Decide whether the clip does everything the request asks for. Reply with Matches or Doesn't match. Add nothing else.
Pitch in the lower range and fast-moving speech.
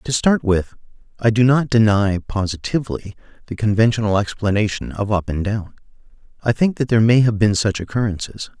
Doesn't match